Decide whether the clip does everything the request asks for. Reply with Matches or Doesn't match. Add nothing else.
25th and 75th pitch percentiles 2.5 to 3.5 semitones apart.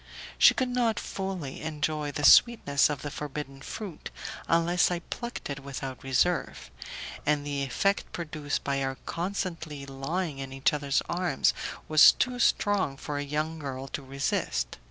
Doesn't match